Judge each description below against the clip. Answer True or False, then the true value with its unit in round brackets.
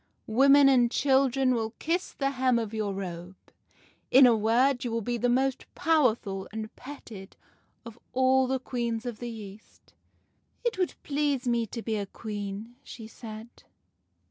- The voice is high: True (240 Hz)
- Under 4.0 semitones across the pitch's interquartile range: True (3.4 semitones)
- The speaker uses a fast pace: False (170 wpm)